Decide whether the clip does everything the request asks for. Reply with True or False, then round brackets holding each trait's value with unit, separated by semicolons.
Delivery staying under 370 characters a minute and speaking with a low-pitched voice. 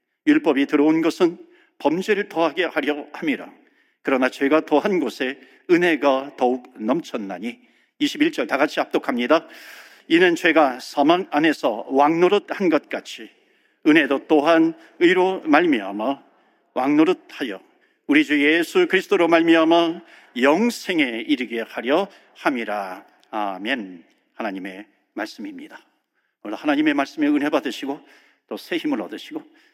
False (270 characters per minute; 265 Hz)